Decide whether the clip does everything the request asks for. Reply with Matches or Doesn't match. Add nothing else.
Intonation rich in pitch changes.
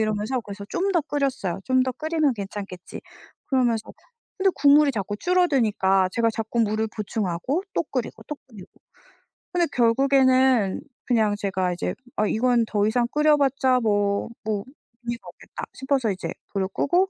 Doesn't match